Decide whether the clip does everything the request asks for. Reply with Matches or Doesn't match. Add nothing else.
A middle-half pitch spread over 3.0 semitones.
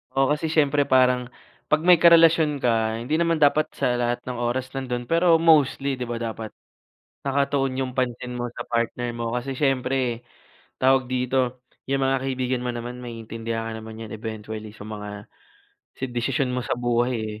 Doesn't match